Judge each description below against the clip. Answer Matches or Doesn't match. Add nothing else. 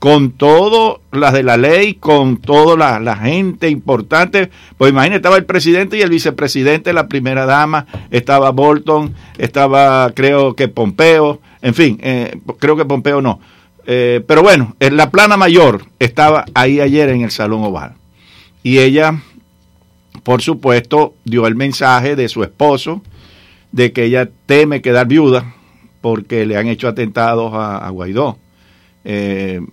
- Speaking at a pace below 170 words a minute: Matches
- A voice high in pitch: Doesn't match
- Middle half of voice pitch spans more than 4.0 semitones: Matches